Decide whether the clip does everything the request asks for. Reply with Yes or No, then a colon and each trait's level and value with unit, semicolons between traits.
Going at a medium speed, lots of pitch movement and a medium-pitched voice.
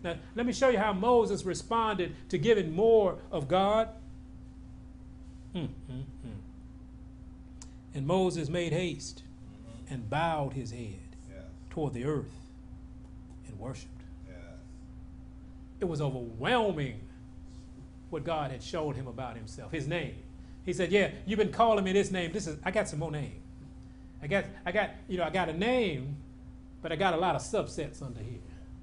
Yes: average, 150 wpm; wide, 7.6 semitones; medium, 155 Hz